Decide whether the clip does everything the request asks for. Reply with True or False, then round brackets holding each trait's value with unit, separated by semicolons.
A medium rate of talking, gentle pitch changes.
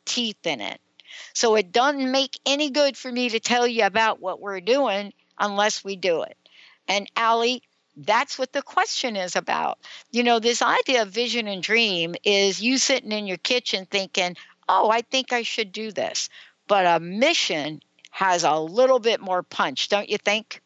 False (185 wpm; 4.2 semitones)